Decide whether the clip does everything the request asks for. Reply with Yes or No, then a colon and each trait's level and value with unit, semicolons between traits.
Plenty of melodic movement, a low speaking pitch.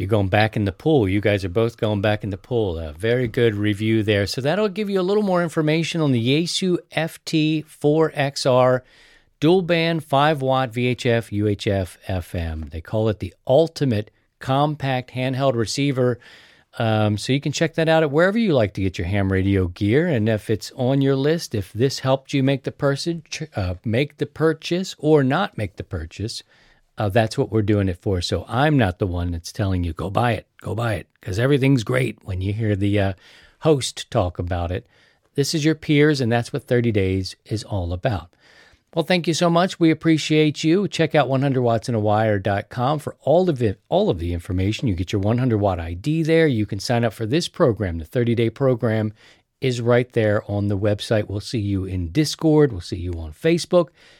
Yes: wide, 6.4 semitones; low, 120 Hz